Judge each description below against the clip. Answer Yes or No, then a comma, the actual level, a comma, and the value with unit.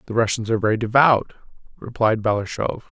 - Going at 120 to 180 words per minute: Yes, average, 140 wpm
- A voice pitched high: No, low, 115 Hz